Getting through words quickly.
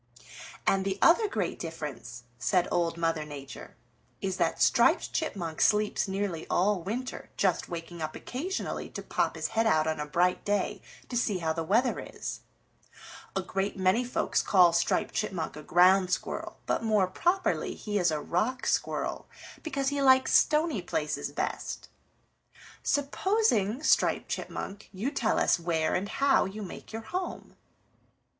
No: average, 155 wpm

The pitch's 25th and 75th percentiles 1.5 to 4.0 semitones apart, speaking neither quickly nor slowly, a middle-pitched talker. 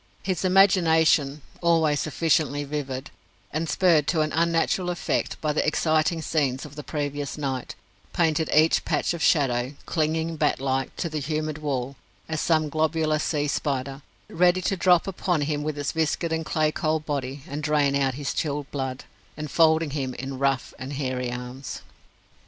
Yes: narrow, 2.6 semitones; average, 165 wpm; medium, 150 Hz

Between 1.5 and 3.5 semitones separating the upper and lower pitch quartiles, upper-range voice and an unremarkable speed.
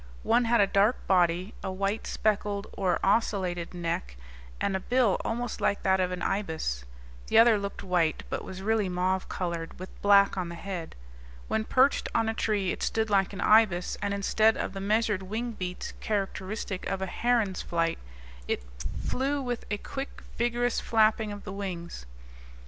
Yes: average, 3.2 semitones; high, 200 Hz; average, 175 wpm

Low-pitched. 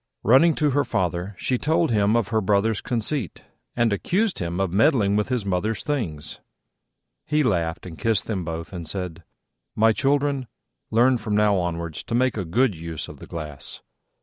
Yes: low, 105 Hz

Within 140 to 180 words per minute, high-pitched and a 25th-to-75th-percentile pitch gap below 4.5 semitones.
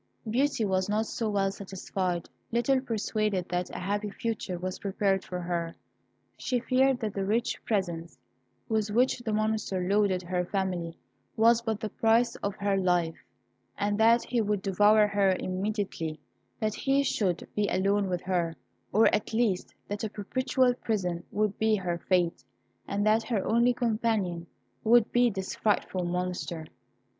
Yes: average, 155 wpm; high, 205 Hz; average, 3.3 semitones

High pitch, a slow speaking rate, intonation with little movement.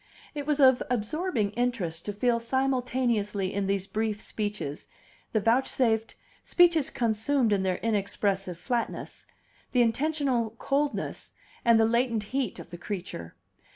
No: high, 225 Hz; slow, 130 wpm; average, 4.2 semitones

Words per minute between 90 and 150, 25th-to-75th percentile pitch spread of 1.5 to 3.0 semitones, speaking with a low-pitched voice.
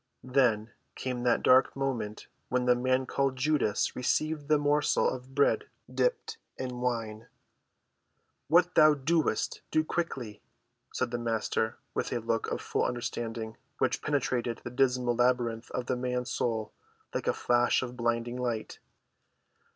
Yes: average, 145 wpm; narrow, 2.5 semitones; low, 125 Hz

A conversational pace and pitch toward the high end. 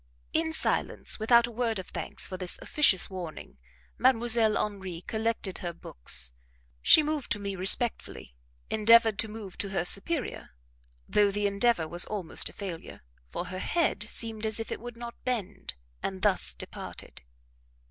Yes: average, 160 wpm; high, 210 Hz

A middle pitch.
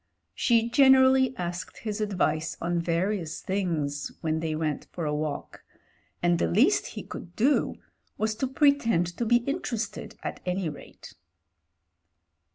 Yes: medium, 180 Hz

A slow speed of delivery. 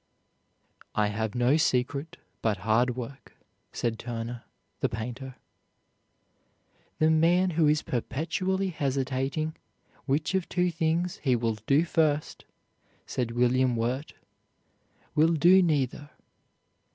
Yes: slow, 110 wpm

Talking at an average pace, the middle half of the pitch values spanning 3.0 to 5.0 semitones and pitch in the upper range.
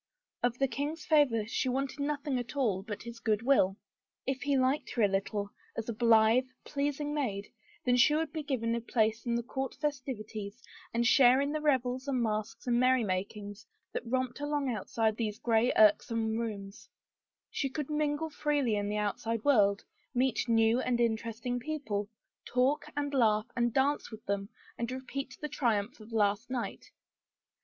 Yes: average, 170 wpm; average, 3.9 semitones; high, 240 Hz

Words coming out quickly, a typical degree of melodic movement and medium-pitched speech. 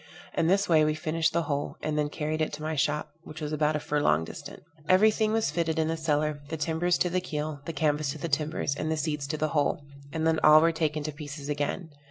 No: fast, 255 wpm; narrow, 1.5 semitones; medium, 155 Hz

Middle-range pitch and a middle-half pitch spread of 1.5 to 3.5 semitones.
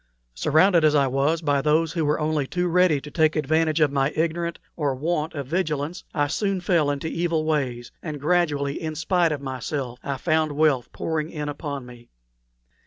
Yes: medium, 155 Hz; narrow, 2.5 semitones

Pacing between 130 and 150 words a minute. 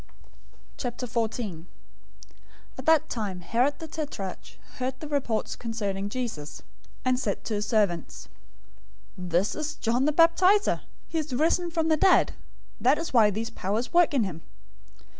Yes: average, 145 wpm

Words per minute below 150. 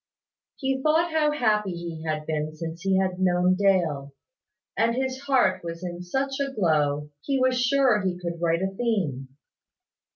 No: average, 165 wpm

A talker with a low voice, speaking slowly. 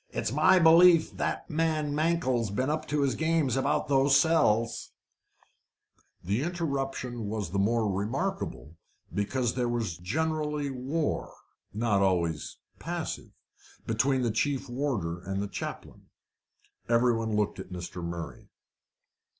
Yes: low, 125 Hz; slow, 125 wpm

